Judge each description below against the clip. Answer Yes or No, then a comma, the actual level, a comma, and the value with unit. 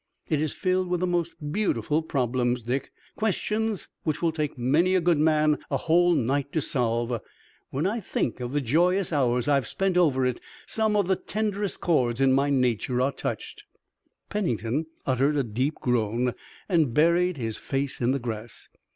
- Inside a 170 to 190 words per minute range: Yes, average, 175 wpm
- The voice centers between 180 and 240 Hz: No, medium, 145 Hz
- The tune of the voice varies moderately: No, wide, 5.9 semitones